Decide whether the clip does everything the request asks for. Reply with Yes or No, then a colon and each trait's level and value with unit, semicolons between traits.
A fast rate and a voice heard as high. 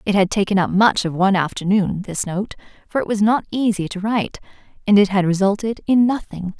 Yes: fast, 210 wpm; high, 200 Hz